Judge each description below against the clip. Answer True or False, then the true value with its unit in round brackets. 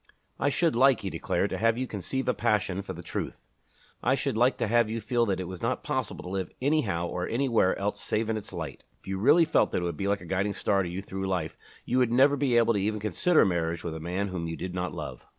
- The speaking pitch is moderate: False (100 Hz)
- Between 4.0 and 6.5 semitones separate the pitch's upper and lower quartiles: True (4.7 semitones)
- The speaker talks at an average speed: False (270 wpm)